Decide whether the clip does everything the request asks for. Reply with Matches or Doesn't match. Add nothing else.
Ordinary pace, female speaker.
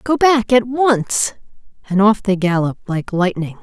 Matches